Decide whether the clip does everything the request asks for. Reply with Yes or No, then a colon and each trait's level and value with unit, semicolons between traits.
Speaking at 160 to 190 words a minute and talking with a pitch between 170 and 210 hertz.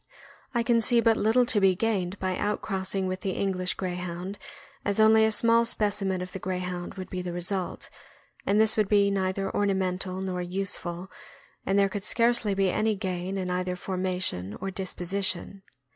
Yes: average, 180 wpm; high, 190 Hz